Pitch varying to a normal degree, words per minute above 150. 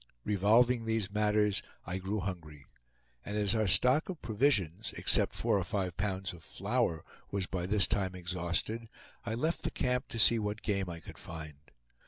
Yes: average, 3.6 semitones; average, 175 wpm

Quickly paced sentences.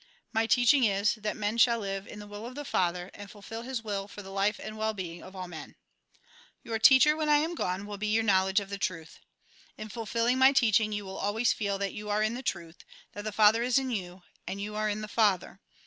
Yes: fast, 250 wpm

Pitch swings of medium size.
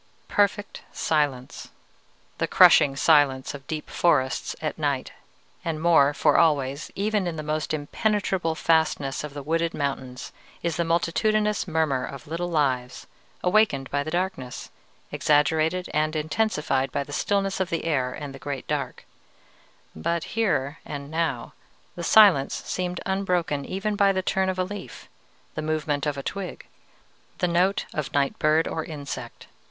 Yes: average, 4.2 semitones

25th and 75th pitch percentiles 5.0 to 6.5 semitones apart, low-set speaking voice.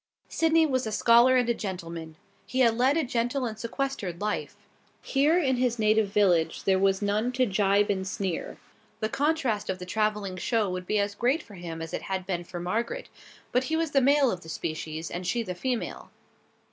No: wide, 5.4 semitones; high, 215 Hz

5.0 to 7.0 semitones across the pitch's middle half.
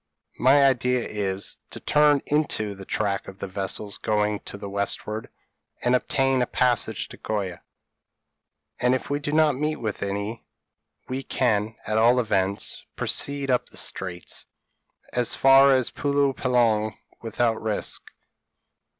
No: average, 4.5 semitones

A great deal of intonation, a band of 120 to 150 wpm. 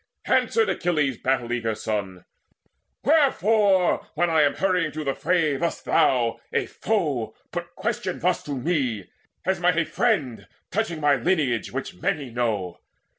Yes: wide, 6.6 semitones; average, 145 wpm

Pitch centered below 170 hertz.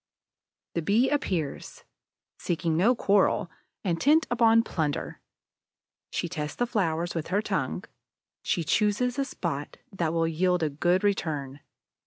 No: medium, 180 Hz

